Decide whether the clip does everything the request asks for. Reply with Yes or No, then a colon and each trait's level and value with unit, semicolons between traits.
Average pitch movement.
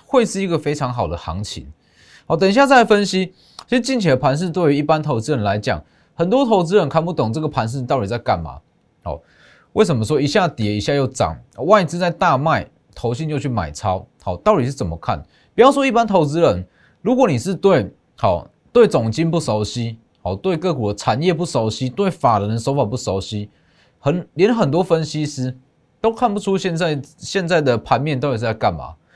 No: wide, 8.0 semitones